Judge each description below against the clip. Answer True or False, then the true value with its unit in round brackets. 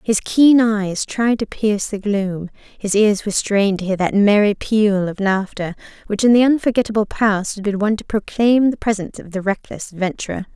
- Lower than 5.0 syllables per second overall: False (5.2 syllables/s)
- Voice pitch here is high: True (205 Hz)